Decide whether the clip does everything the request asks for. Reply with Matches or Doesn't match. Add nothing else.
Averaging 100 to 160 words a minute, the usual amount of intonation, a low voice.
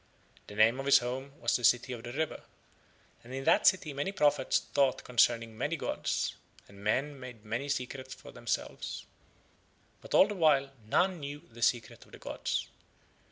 Doesn't match